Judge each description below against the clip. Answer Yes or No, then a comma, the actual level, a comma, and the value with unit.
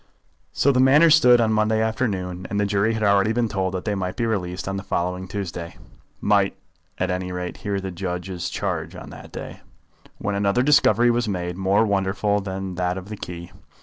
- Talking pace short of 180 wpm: No, fast, 205 wpm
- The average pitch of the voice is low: Yes, low, 100 Hz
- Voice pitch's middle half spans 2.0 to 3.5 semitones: Yes, average, 3.2 semitones